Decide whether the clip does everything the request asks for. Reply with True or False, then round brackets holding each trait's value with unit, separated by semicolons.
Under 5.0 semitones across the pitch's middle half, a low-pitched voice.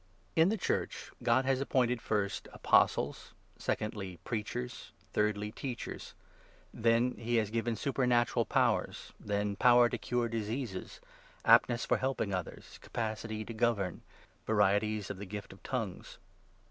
True (2.9 semitones; 115 Hz)